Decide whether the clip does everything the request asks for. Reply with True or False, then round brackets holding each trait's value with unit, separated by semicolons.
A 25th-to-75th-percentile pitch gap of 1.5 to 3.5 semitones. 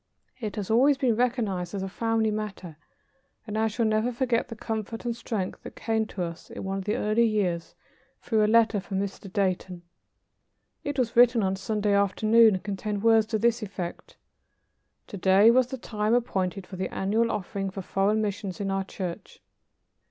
True (2.9 semitones)